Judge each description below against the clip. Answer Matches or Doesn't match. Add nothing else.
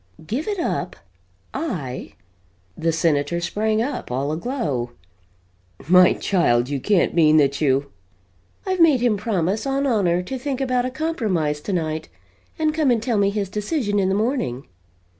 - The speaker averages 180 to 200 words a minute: Doesn't match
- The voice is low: Doesn't match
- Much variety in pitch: Matches